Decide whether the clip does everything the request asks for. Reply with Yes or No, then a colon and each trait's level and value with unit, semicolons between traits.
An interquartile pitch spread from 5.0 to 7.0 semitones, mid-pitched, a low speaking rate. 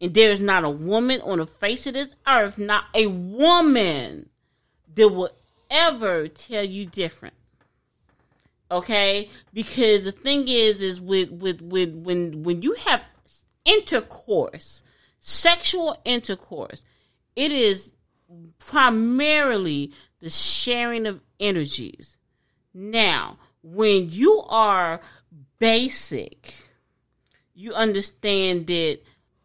No: wide, 5.6 semitones; high, 205 Hz; slow, 105 wpm